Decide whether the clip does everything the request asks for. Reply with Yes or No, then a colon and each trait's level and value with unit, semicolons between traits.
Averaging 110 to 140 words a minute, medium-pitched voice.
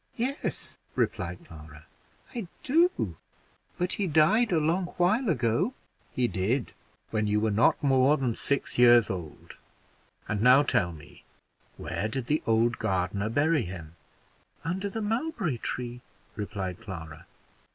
No: slow, 135 wpm; low, 120 Hz